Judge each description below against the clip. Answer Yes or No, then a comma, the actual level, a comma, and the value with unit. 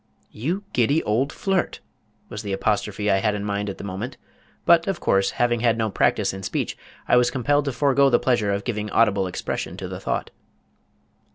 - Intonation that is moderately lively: Yes, average, 4.6 semitones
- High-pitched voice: No, low, 115 Hz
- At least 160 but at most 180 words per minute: No, average, 195 wpm